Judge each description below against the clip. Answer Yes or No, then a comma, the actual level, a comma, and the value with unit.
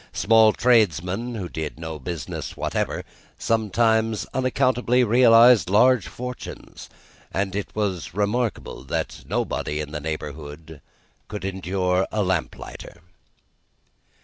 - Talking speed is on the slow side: Yes, slow, 105 wpm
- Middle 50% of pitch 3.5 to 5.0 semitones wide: No, wide, 5.6 semitones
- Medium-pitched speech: No, low, 100 Hz